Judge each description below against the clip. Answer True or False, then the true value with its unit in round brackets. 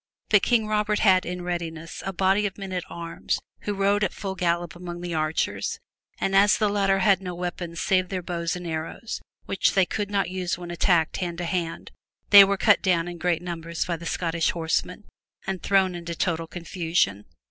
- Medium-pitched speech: True (180 Hz)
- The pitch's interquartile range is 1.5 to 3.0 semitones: True (2.5 semitones)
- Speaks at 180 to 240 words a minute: True (200 wpm)